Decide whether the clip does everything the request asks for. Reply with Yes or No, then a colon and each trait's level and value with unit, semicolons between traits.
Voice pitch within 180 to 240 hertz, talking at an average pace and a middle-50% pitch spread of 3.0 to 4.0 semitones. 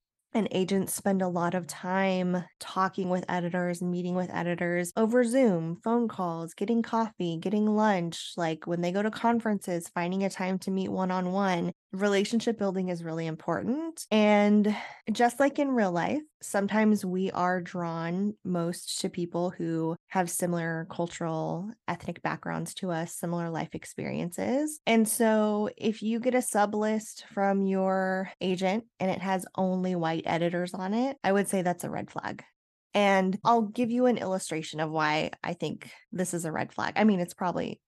Yes: high, 190 Hz; average, 175 wpm; average, 3.5 semitones